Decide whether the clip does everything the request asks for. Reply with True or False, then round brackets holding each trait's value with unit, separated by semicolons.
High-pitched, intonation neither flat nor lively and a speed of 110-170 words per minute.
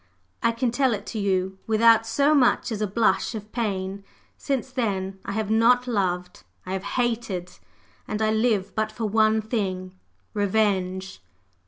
True (215 Hz; 3.2 semitones; 160 wpm)